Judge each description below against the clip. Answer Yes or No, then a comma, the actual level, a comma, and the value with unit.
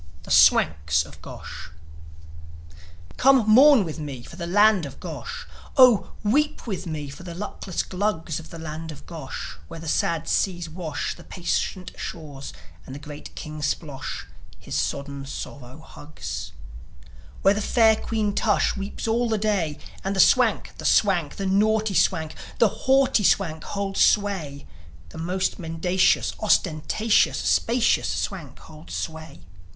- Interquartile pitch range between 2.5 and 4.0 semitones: No, average, 5.3 semitones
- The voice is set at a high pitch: No, medium, 175 Hz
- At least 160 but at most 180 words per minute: No, average, 145 wpm